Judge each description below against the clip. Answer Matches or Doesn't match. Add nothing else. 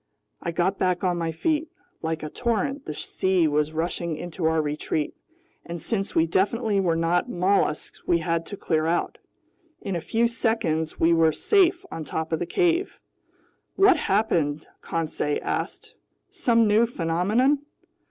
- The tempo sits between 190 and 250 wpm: Doesn't match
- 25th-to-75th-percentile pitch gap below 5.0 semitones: Doesn't match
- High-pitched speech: Doesn't match